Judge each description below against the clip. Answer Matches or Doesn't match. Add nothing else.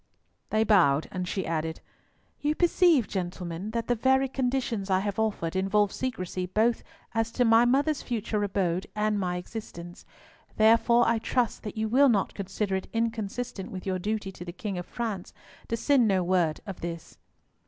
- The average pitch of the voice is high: Matches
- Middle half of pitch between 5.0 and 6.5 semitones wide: Doesn't match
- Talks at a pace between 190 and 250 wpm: Doesn't match